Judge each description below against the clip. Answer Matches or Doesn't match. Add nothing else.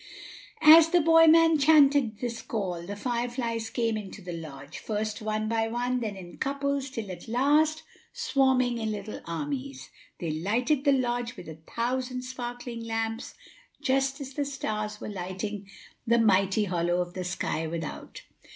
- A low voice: Doesn't match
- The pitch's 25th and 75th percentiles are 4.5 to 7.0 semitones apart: Matches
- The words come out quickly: Doesn't match